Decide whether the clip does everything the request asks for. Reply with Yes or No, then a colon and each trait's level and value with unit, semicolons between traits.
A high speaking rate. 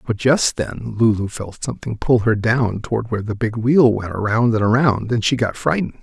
Yes: fast, 220 wpm